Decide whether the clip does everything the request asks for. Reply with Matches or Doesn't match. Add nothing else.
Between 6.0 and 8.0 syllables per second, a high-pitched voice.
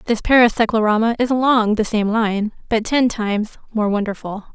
Doesn't match